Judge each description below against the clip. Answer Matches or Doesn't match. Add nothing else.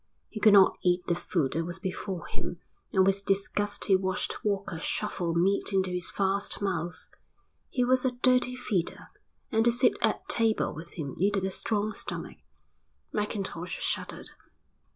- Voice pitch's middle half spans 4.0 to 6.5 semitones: Doesn't match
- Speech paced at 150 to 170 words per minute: Matches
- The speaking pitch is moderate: Doesn't match